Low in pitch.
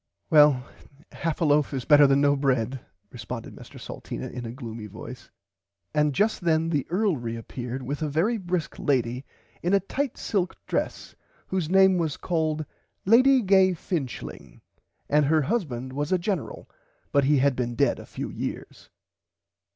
No: medium, 150 Hz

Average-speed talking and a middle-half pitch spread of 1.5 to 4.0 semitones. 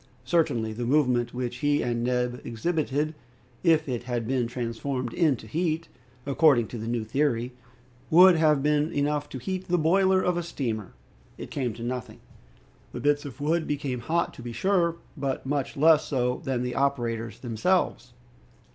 No: average, 165 wpm; average, 4.5 semitones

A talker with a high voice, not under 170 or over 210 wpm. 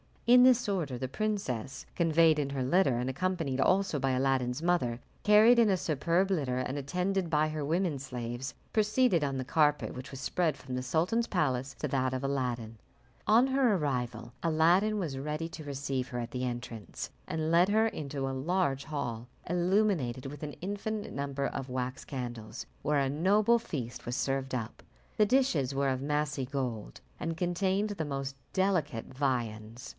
No: medium, 145 Hz; average, 175 wpm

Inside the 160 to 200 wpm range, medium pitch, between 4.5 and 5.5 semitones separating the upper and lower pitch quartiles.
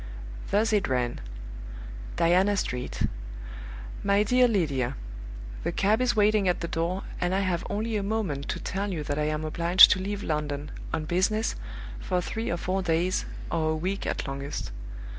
Yes: average, 170 wpm; medium, 180 Hz; average, 4.8 semitones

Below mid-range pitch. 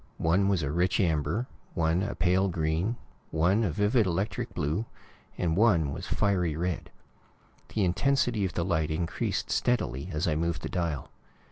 Yes: very low, 90 Hz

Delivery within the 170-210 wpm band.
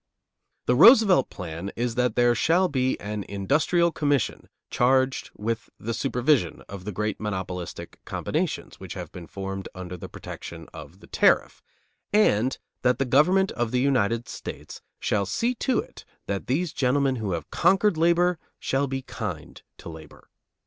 No: average, 155 wpm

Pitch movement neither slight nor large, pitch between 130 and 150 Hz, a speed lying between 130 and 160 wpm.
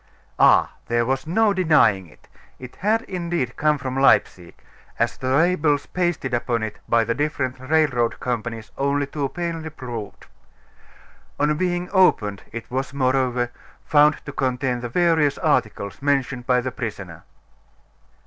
Yes: average, 4.5 semitones; low, 135 Hz; average, 140 wpm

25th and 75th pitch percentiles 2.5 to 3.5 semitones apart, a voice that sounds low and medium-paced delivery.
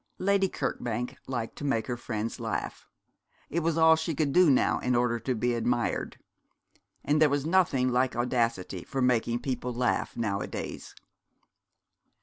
No: average, 4.0 semitones; low, 125 Hz; average, 150 wpm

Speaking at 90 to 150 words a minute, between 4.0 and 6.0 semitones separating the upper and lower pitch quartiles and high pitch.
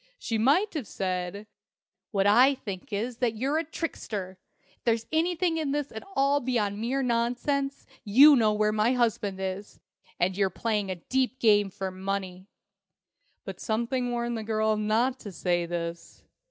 No: average, 165 wpm; average, 4.7 semitones; high, 220 Hz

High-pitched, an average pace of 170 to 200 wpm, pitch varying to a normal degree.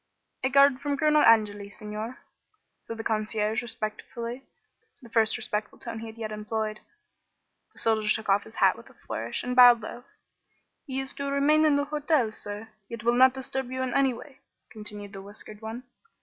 Yes: high, 230 Hz; average, 185 wpm; average, 3.6 semitones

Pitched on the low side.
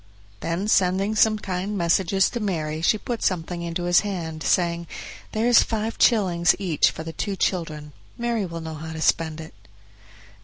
No: medium, 175 Hz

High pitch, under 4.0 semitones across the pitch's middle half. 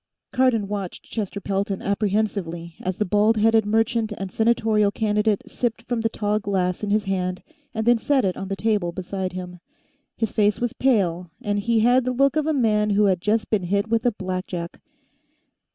Yes: high, 210 Hz; average, 2.8 semitones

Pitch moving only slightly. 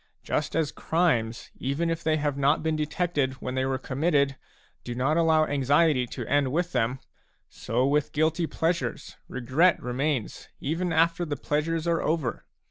No: average, 3.7 semitones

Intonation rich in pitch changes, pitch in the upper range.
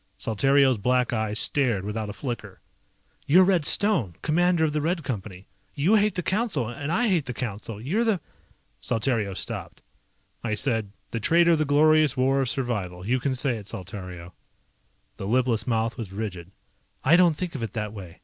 No: wide, 6.5 semitones; low, 125 Hz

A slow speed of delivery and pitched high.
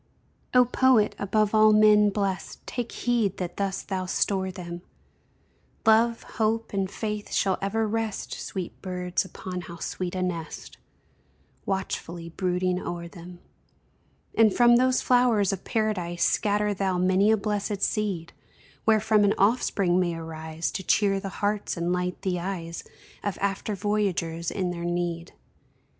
No: average, 145 wpm; high, 195 Hz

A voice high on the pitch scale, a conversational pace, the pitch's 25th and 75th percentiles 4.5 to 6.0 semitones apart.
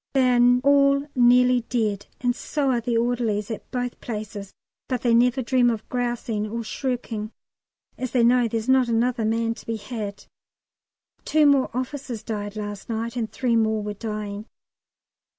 No: high, 235 Hz; average, 165 wpm; narrow, 2.4 semitones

